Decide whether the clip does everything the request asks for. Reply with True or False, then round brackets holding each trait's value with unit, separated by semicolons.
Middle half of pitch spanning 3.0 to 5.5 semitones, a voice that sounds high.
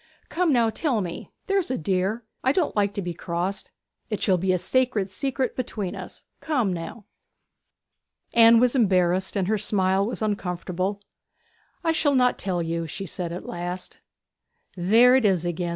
True (5.2 semitones; 200 Hz)